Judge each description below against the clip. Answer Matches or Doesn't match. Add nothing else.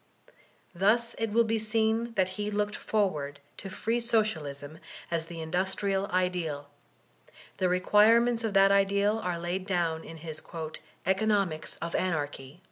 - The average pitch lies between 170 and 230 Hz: Matches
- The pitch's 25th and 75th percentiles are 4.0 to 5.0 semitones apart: Matches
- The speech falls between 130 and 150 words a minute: Matches